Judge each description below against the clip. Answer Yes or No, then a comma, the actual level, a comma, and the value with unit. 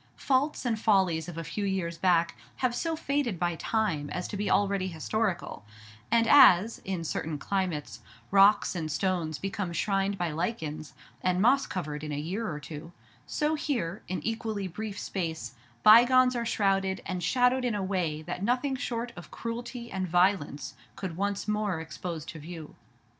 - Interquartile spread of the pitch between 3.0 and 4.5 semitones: No, average, 5.2 semitones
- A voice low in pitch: No, high, 190 Hz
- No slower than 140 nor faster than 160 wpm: No, average, 170 wpm